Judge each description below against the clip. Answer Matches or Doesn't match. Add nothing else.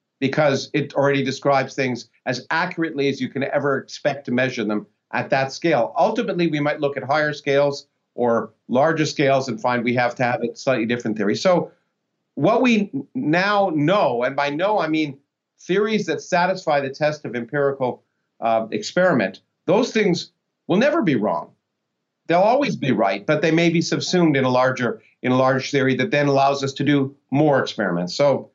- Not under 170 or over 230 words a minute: Matches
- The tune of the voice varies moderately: Matches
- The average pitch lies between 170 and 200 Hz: Doesn't match